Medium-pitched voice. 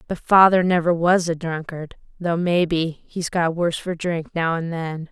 Yes: medium, 170 Hz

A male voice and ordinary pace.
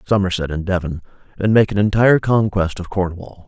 Yes: male; average, 175 wpm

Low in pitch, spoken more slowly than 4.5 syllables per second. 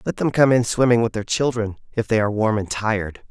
No: low, 110 Hz; 5.9 syllables/s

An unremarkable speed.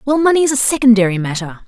No: fast, 215 wpm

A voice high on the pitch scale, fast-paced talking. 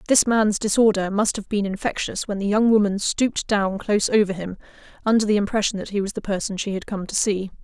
Yes: high, 205 Hz; fast, 230 wpm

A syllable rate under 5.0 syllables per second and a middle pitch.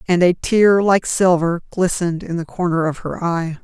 Yes: 4.8 syllables/s; medium, 175 Hz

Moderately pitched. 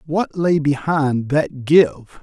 Yes: medium, 145 Hz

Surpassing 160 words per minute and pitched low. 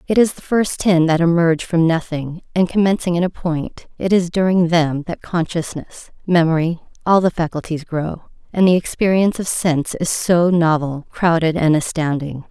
No: average, 170 wpm; medium, 170 Hz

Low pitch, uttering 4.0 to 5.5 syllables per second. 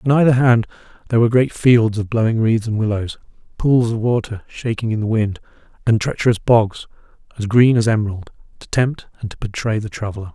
No: low, 110 Hz; 5.8 syllables/s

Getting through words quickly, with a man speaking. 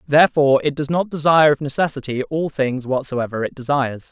No: average, 175 wpm; male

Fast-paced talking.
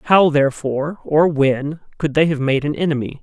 No: average, 185 wpm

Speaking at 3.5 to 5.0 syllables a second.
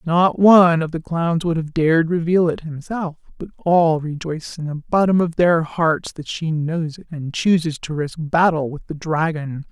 Yes: 4.6 syllables/s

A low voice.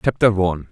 Yes: very low, 95 Hz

